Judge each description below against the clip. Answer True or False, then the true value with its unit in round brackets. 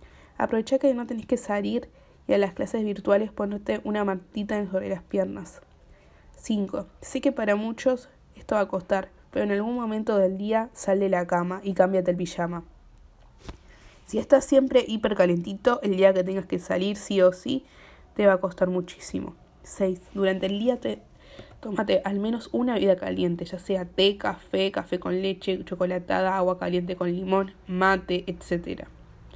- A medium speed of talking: True (170 wpm)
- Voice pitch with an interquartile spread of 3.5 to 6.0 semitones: False (2.9 semitones)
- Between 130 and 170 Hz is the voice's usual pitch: False (195 Hz)